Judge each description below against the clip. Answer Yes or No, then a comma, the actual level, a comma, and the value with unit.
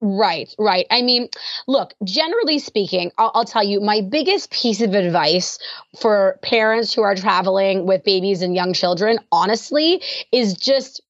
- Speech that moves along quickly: No, average, 155 wpm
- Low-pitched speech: No, high, 215 Hz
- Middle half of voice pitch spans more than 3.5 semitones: Yes, average, 4.2 semitones